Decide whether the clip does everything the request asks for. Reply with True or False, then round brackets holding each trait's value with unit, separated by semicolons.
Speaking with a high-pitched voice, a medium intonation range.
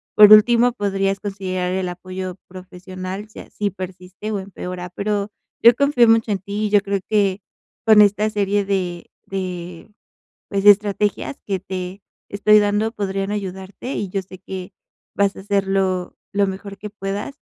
False (195 Hz; 1.8 semitones)